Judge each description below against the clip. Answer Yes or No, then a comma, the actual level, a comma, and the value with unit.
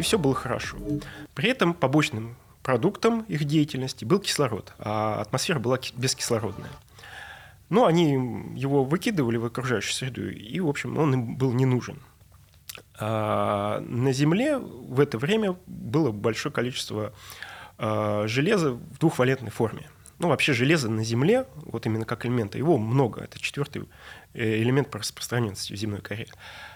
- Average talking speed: Yes, average, 140 wpm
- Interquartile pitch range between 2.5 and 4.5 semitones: No, average, 5.2 semitones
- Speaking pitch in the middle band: No, low, 130 Hz